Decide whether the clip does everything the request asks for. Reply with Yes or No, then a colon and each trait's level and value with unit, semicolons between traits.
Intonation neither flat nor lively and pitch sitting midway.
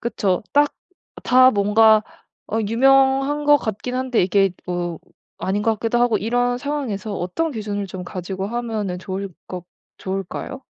No: average, 4.7 semitones; high, 220 Hz